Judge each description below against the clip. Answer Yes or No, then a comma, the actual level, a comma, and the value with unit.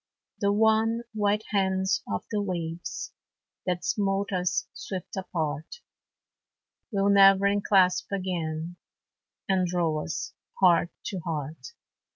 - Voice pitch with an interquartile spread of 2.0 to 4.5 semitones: Yes, average, 2.9 semitones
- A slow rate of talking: Yes, slow, 110 wpm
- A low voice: No, high, 190 Hz